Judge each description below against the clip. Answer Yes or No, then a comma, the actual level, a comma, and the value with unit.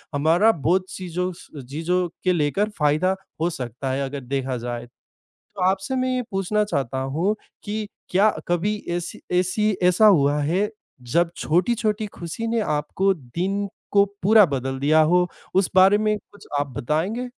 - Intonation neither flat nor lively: No, wide, 5.8 semitones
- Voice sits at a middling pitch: Yes, medium, 180 Hz